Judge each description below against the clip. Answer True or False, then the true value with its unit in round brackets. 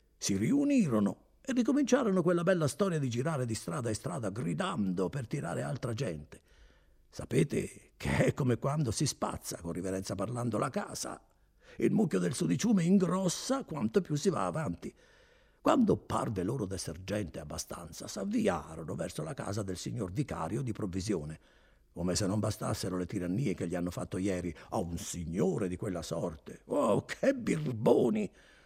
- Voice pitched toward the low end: True (105 Hz)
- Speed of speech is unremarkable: True (155 wpm)